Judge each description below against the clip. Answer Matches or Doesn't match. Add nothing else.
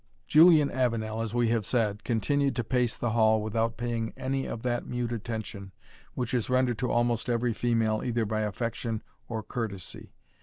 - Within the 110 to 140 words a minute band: Doesn't match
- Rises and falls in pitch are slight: Matches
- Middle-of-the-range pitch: Doesn't match